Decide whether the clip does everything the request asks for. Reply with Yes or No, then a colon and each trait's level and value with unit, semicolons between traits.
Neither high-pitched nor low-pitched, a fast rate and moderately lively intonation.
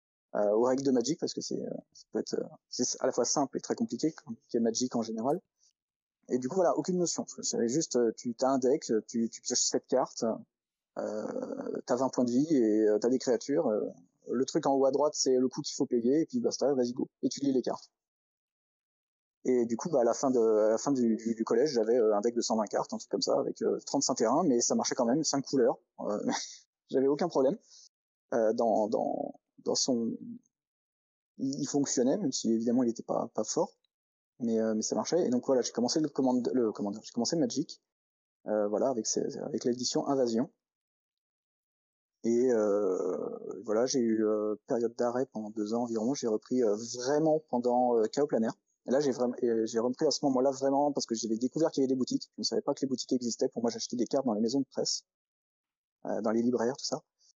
No: low, 125 Hz; fast, 230 wpm; average, 3.6 semitones